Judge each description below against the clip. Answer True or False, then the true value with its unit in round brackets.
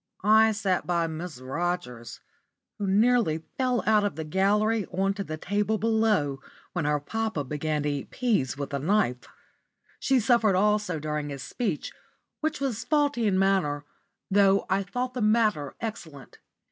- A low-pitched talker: False (195 Hz)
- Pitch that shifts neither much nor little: False (6.3 semitones)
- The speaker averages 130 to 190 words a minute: True (160 wpm)